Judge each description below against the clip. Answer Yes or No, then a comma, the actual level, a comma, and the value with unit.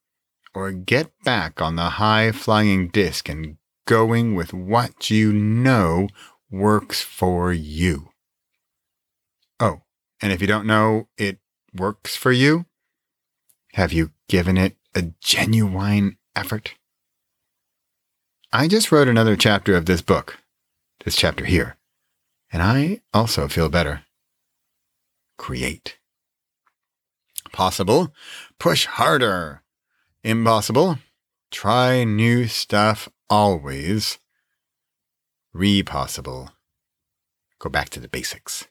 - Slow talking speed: Yes, slow, 100 wpm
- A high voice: No, low, 100 Hz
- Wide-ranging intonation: No, average, 4.2 semitones